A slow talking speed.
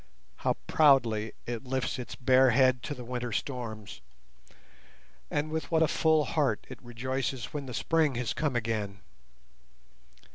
No: average, 145 wpm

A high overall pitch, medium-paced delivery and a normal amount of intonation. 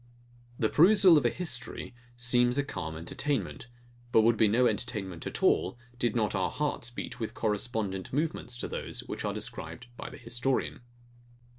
No: low, 120 Hz; average, 165 wpm; average, 3.9 semitones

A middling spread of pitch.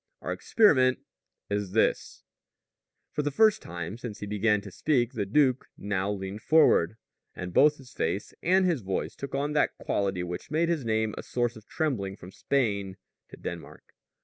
No: wide, 6.7 semitones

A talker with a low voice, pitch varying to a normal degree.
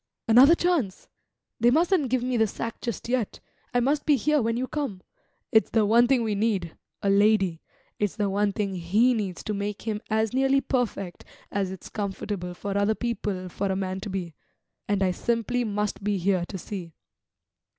No: high, 210 Hz; average, 3.8 semitones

